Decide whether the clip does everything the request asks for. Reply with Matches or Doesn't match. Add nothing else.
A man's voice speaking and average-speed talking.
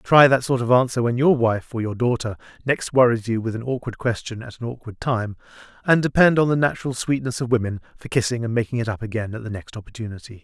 Doesn't match